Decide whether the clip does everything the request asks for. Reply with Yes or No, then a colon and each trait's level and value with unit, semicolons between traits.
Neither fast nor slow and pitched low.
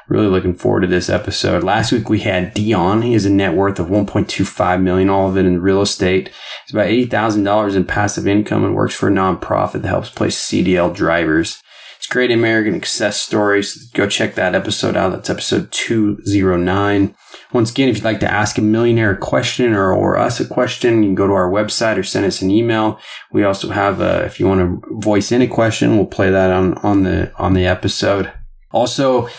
No: fast, 220 wpm; low, 105 Hz